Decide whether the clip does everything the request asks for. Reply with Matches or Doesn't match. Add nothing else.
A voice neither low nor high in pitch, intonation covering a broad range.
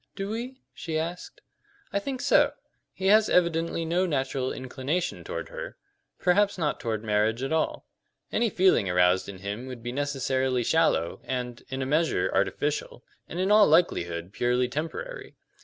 Matches